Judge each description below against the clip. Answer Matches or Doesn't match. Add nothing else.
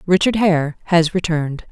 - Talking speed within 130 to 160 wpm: Matches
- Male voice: Doesn't match